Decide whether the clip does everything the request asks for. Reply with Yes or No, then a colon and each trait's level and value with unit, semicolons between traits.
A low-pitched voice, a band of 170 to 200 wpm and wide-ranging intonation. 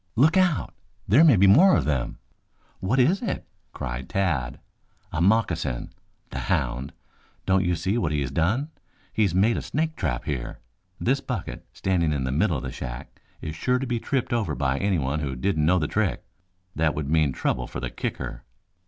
Yes: very low, 90 Hz; average, 190 wpm; wide, 8.7 semitones